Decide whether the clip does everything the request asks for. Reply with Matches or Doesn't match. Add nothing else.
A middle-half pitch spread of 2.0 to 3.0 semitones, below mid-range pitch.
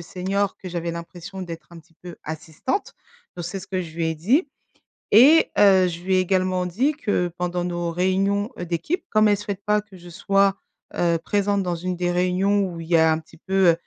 Doesn't match